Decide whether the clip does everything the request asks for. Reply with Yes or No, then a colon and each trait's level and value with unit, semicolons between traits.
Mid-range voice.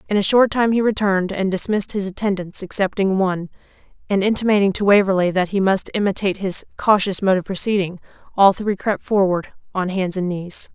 No: high, 195 Hz